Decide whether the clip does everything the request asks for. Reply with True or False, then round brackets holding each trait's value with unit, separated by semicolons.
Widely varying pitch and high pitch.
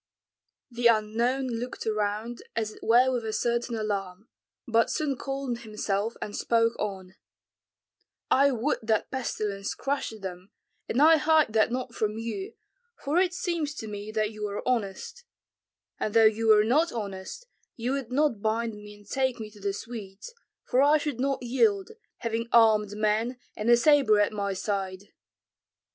False (3.7 semitones; 230 Hz)